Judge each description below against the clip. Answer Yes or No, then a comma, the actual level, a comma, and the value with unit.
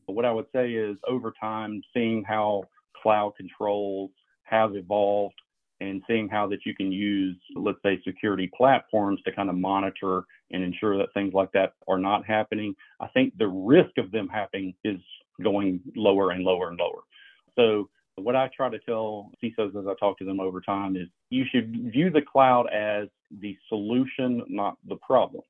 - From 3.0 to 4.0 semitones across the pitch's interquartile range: No, narrow, 2.4 semitones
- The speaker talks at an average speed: Yes, average, 185 wpm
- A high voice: No, low, 105 Hz